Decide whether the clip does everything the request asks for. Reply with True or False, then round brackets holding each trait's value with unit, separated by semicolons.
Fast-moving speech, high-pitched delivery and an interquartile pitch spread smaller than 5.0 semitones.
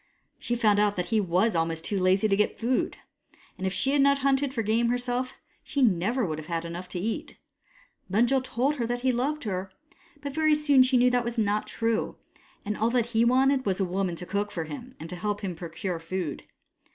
False (230 wpm; 220 Hz; 5.4 semitones)